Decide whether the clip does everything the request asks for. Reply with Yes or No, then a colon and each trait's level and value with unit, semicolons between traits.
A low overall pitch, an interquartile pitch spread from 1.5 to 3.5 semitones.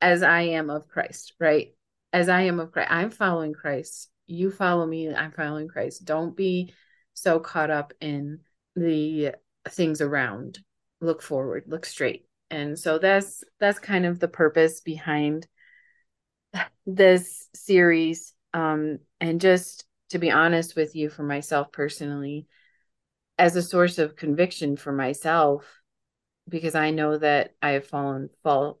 No: medium, 160 Hz; average, 2.9 semitones